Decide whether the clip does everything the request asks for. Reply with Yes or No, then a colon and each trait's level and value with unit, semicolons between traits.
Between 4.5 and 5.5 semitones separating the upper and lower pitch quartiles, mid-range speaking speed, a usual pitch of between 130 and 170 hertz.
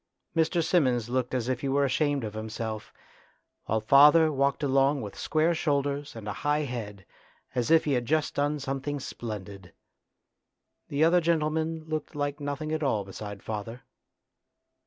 Yes: average, 4.8 semitones; average, 155 wpm; medium, 140 Hz